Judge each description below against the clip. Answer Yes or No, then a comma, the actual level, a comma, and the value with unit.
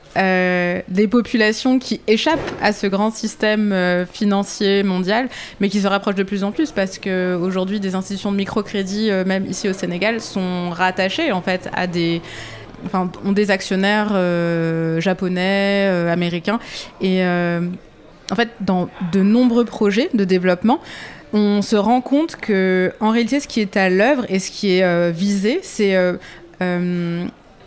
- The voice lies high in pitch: Yes, high, 195 Hz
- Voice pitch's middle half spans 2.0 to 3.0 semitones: Yes, average, 2.7 semitones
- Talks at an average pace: Yes, average, 165 wpm